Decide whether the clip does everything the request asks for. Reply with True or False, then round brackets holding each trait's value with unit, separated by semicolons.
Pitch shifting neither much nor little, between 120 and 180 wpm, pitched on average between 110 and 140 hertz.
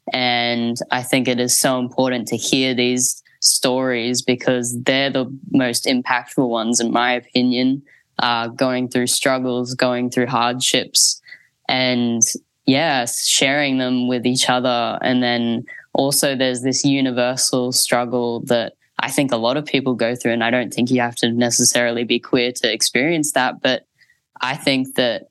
False (1.2 semitones; 160 wpm; 125 Hz)